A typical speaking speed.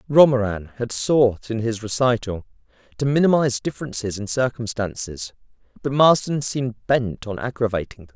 No: slow, 130 wpm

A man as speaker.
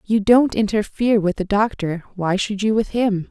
No: female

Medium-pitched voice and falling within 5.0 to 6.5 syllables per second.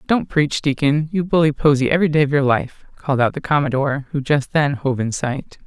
Yes: medium, 145 Hz; 5.7 syllables/s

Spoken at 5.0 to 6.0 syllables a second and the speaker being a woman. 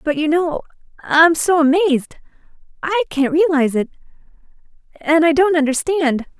Yes: 5.1 syllables/s; female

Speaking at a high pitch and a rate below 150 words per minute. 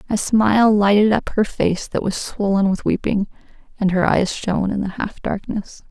No: high, 200 Hz; average, 195 wpm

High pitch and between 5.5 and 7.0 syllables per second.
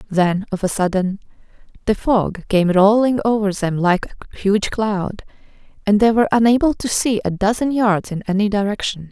No: high, 205 Hz; 5.0 syllables/s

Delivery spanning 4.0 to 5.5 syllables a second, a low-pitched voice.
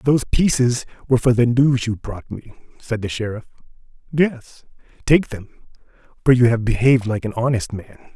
Yes: 5.3 syllables/s; low, 120 Hz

